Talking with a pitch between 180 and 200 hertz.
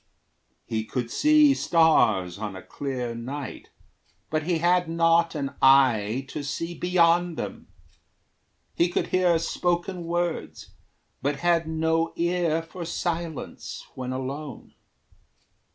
No: medium, 160 Hz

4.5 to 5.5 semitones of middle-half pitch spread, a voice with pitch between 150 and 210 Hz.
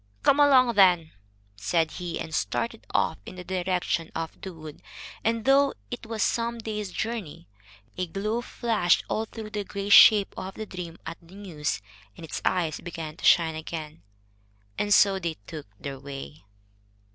Yes: average, 5.1 semitones; medium, 185 Hz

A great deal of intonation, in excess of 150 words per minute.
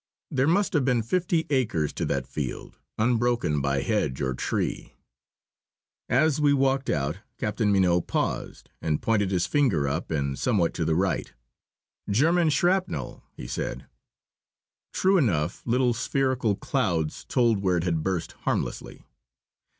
No: wide, 8.3 semitones; average, 140 wpm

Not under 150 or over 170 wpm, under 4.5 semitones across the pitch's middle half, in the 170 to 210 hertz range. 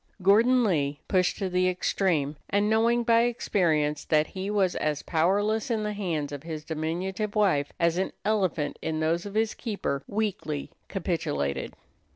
No: average, 160 wpm; average, 5.1 semitones; medium, 185 Hz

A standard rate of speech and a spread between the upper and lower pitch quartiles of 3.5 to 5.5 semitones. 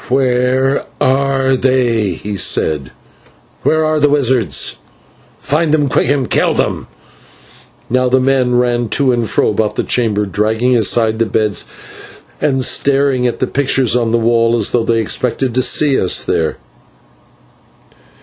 No: average, 150 wpm; average, 2.8 semitones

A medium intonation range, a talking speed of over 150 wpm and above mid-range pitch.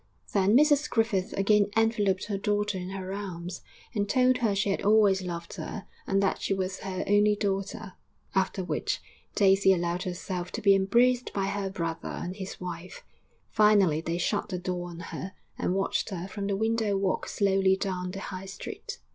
No: narrow, 1.9 semitones; average, 180 wpm; high, 195 Hz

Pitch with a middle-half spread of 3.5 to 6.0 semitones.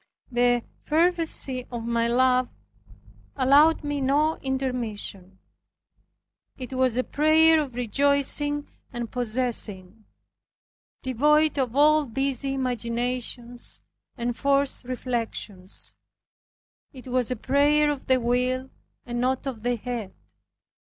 No: average, 2.8 semitones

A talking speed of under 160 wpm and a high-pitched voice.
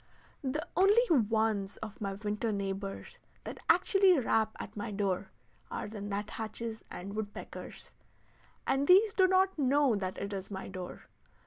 Yes: average, 150 wpm; high, 215 Hz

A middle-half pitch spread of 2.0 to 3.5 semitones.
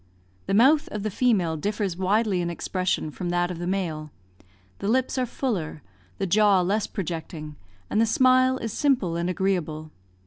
No: average, 4.4 semitones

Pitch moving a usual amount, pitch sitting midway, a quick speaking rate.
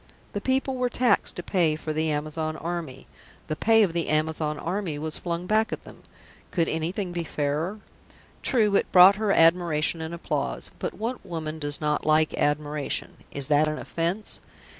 No: average, 4.2 semitones; medium, 165 Hz; average, 175 wpm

